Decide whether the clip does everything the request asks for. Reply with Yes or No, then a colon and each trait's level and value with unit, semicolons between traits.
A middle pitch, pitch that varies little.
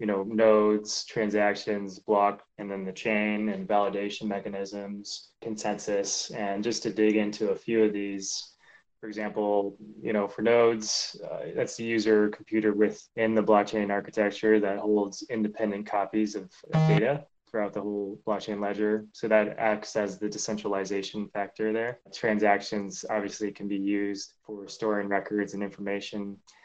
No: low, 105 Hz; narrow, 1.2 semitones